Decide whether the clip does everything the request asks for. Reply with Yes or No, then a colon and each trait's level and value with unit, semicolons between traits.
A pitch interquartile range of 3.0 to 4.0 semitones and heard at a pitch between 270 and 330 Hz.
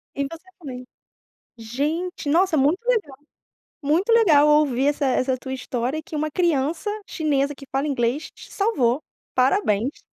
Yes: average, 3.7 semitones; very high, 290 Hz